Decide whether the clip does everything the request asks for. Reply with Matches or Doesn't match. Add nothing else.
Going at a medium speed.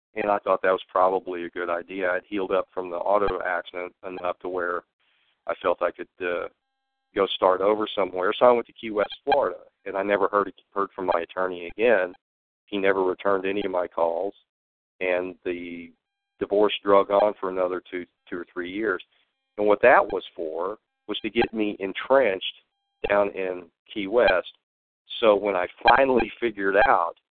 Matches